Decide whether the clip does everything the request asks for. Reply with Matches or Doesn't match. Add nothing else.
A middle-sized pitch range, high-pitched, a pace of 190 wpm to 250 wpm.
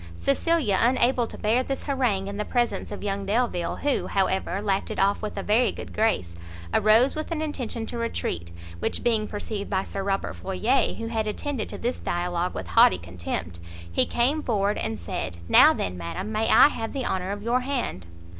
Matches